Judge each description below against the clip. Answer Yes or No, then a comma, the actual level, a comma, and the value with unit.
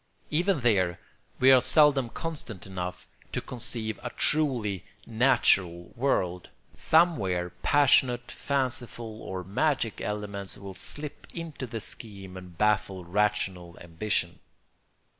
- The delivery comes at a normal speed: No, slow, 110 wpm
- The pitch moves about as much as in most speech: No, wide, 6.1 semitones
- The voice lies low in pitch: Yes, low, 110 Hz